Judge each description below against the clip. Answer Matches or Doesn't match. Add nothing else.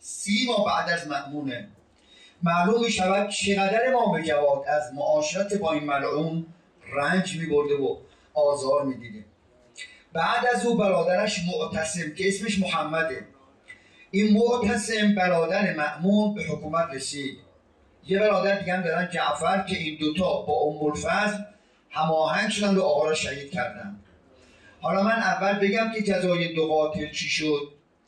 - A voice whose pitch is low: Doesn't match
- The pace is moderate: Matches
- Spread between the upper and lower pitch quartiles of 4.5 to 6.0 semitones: Matches